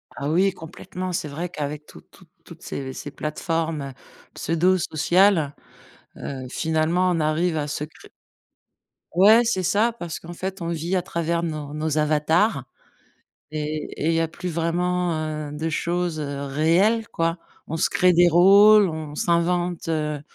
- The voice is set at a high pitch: No, medium, 165 Hz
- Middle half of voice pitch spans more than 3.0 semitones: No, average, 2.7 semitones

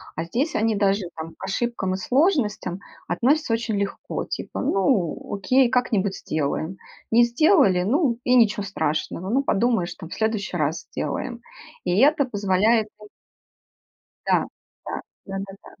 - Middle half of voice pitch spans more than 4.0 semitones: Yes, average, 4.5 semitones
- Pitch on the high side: Yes, high, 210 Hz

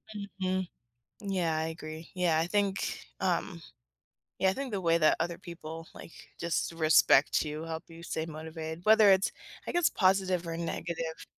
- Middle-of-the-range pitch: Yes, medium, 170 Hz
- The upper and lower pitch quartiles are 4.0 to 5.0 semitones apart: No, average, 2.7 semitones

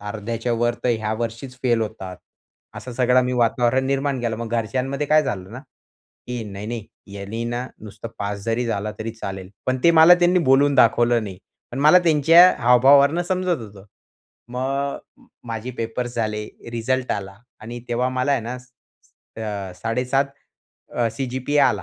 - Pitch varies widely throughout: No, average, 3.2 semitones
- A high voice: No, low, 120 Hz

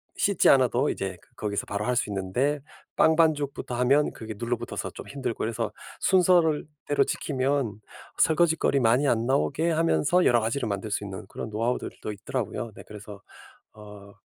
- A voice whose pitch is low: Yes, low, 125 Hz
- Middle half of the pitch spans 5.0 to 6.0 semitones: Yes, wide, 5.4 semitones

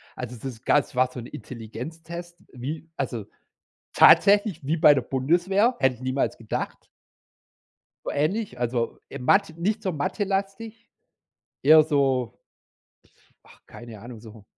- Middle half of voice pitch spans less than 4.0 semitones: No, wide, 6.0 semitones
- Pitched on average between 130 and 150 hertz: Yes, medium, 140 Hz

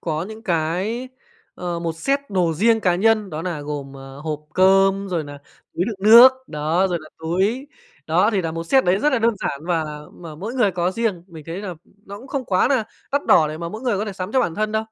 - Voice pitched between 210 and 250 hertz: No, medium, 185 Hz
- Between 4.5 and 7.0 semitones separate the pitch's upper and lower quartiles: Yes, average, 4.9 semitones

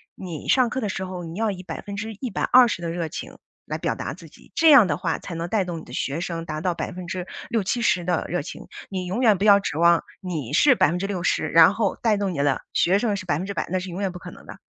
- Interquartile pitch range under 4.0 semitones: Yes, average, 3.3 semitones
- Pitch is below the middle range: No, medium, 185 Hz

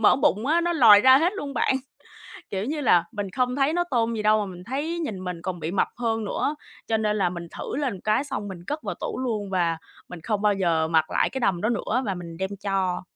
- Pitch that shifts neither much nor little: No, wide, 6.1 semitones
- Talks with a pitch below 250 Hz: Yes, high, 215 Hz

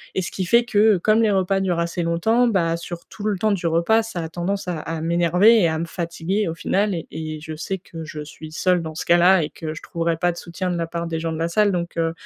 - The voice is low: No, medium, 170 Hz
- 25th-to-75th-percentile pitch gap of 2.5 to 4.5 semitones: Yes, average, 2.8 semitones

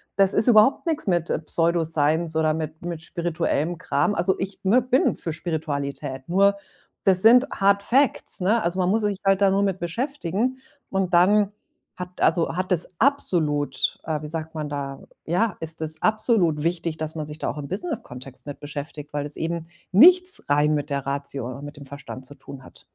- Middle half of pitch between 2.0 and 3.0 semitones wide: No, average, 4.9 semitones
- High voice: No, medium, 170 Hz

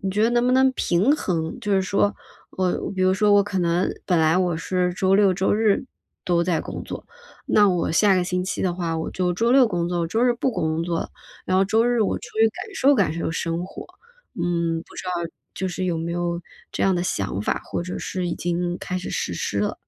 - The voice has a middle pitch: Yes, medium, 180 Hz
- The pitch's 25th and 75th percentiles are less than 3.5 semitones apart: Yes, average, 3.0 semitones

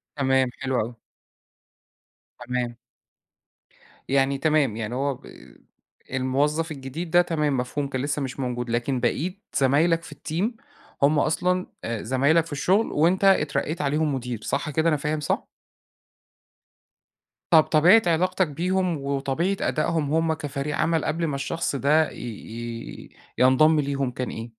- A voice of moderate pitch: Yes, medium, 145 Hz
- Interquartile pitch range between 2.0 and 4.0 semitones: Yes, average, 3.7 semitones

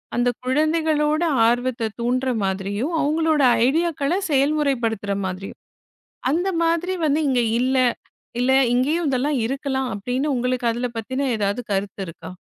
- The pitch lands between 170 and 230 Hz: No, very high, 260 Hz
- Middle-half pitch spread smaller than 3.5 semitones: No, average, 4.1 semitones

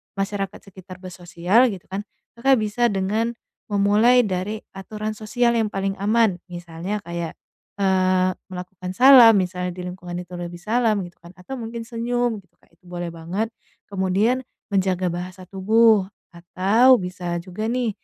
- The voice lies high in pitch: Yes, high, 195 Hz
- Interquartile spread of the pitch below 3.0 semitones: No, average, 3.6 semitones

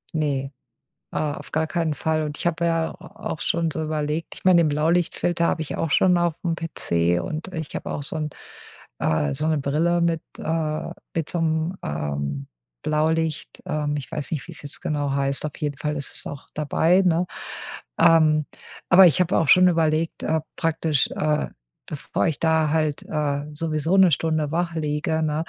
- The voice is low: No, medium, 155 Hz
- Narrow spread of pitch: Yes, narrow, 1.9 semitones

